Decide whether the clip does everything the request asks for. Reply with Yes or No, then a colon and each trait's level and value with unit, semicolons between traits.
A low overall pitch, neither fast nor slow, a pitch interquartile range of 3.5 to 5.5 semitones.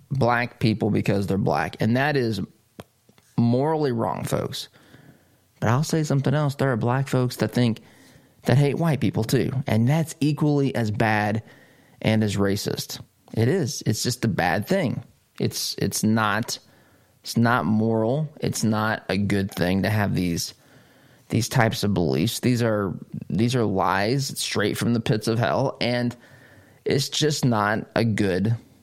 Yes: low, 115 Hz; average, 160 wpm; average, 3.8 semitones